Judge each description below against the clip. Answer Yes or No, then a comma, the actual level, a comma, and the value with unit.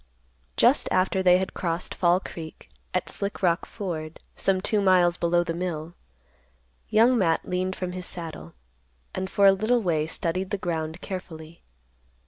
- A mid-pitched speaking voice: Yes, medium, 180 Hz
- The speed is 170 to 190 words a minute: No, average, 155 wpm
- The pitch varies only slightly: Yes, narrow, 2.3 semitones